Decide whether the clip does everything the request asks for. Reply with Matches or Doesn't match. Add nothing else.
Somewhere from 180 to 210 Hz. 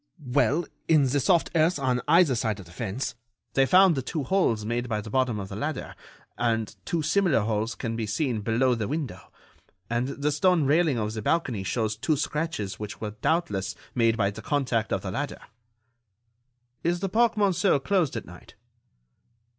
Doesn't match